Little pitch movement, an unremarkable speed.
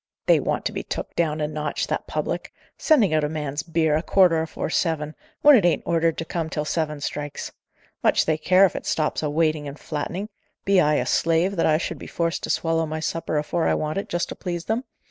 No: narrow, 2.2 semitones; fast, 235 wpm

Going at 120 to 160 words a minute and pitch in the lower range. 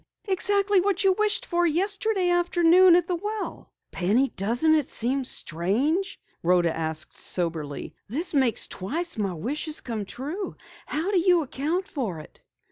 No: average, 150 wpm; very high, 315 Hz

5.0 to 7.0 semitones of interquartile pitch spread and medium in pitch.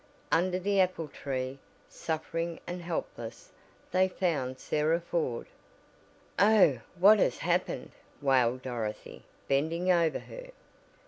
Yes: wide, 5.5 semitones; medium, 165 Hz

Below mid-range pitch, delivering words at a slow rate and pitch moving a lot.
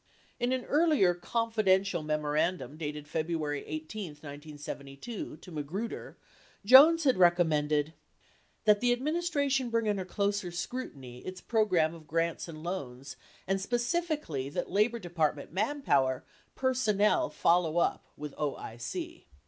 No: medium, 175 Hz; slow, 120 wpm; wide, 7.3 semitones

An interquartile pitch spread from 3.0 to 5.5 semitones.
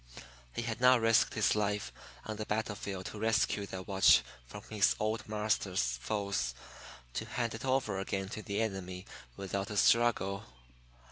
No: narrow, 2.4 semitones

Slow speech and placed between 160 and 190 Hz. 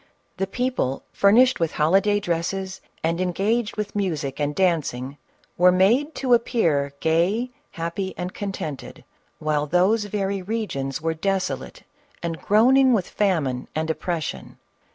Yes: slow, 130 wpm; medium, 185 Hz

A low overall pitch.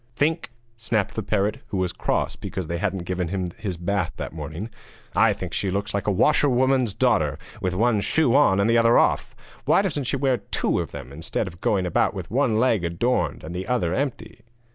Yes: low, 100 Hz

